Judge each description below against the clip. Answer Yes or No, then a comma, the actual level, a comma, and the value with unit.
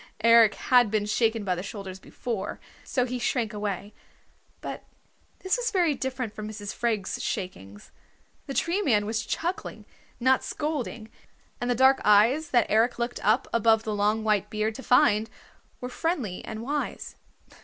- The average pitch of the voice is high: Yes, high, 225 Hz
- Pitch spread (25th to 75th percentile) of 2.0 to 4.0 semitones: Yes, average, 3.5 semitones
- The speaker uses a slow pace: No, average, 160 wpm